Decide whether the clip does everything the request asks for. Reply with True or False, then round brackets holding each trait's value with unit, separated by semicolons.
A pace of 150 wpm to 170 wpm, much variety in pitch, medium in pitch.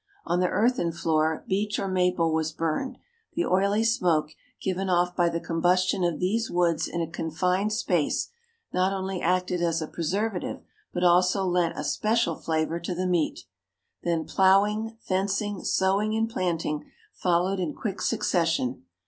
False (155 wpm; 2.7 semitones; 180 Hz)